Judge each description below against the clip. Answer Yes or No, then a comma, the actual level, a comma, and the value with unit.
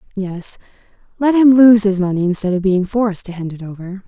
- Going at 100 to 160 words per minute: No, fast, 205 wpm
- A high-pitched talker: Yes, high, 200 Hz